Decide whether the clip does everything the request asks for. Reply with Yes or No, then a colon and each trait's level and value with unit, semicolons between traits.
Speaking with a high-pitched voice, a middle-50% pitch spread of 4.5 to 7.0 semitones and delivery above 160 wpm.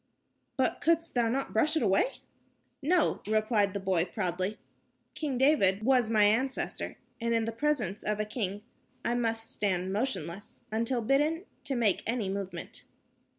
No: high, 225 Hz; average, 4.8 semitones; average, 150 wpm